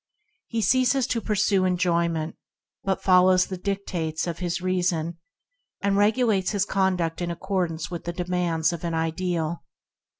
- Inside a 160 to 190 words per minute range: No, average, 145 wpm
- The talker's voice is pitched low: No, medium, 180 Hz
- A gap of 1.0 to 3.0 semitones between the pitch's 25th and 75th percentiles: Yes, narrow, 2.5 semitones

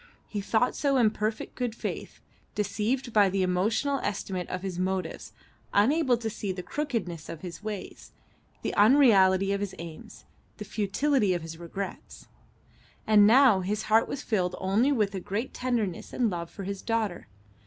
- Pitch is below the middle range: No, high, 205 Hz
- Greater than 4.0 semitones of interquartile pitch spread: No, average, 3.7 semitones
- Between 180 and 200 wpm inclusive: No, average, 165 wpm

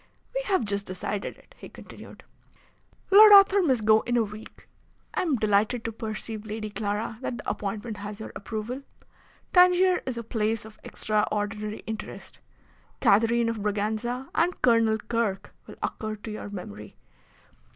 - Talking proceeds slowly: No, average, 150 wpm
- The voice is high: Yes, high, 220 Hz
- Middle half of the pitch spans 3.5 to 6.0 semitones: No, narrow, 2.4 semitones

